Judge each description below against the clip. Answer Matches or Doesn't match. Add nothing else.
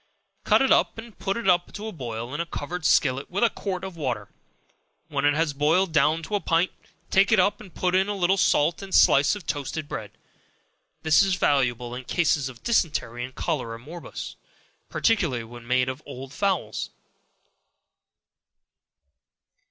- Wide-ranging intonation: Matches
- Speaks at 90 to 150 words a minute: Doesn't match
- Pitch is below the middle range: Doesn't match